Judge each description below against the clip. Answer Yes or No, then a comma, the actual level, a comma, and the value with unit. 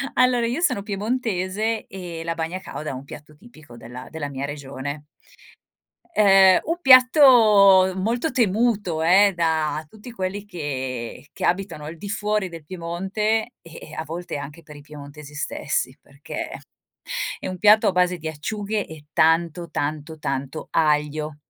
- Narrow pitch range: No, wide, 5.6 semitones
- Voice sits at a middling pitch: Yes, medium, 170 Hz